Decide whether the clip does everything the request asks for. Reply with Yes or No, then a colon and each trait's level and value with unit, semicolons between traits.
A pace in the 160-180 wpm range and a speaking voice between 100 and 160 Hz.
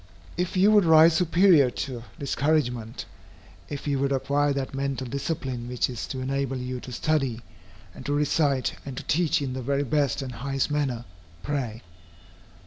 Yes: average, 165 wpm; medium, 140 Hz